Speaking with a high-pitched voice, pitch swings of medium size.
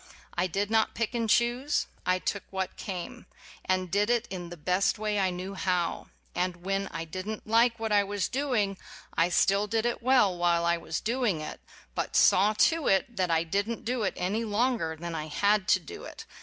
Yes: high, 195 Hz; average, 4.0 semitones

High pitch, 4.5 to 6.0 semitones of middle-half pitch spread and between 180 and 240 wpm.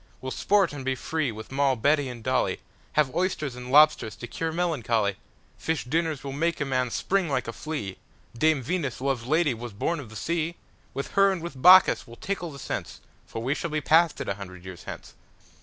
No: medium, 140 Hz; average, 5.2 semitones; average, 190 wpm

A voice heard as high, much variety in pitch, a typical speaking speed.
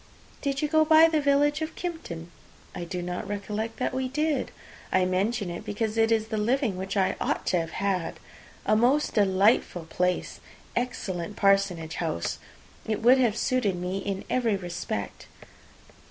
Yes: high, 210 Hz; wide, 5.8 semitones; average, 165 wpm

